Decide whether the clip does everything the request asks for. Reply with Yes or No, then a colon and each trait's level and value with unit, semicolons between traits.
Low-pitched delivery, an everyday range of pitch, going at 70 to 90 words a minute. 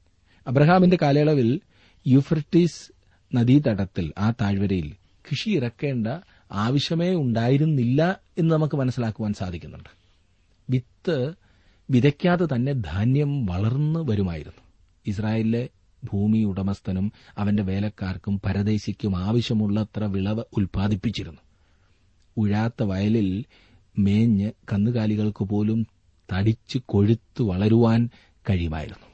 Yes: low, 105 Hz; average, 4.6 semitones; average, 75 wpm